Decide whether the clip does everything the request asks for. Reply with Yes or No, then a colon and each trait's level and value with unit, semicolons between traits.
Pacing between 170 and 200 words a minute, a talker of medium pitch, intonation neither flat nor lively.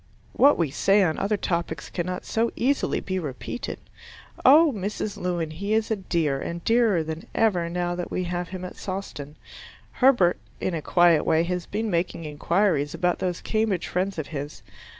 Yes: average, 175 wpm; medium, 180 Hz; average, 3.5 semitones